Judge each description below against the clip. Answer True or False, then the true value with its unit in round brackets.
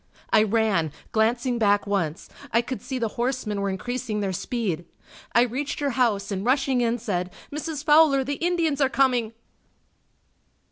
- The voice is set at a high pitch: True (235 Hz)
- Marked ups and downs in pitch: False (4.6 semitones)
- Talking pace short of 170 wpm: True (155 wpm)